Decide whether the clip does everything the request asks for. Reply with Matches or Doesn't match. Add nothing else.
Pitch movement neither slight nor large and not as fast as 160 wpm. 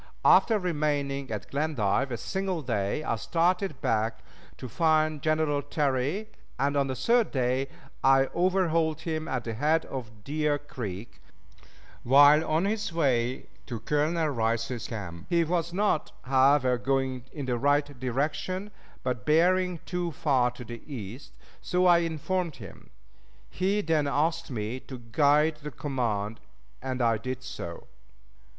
Matches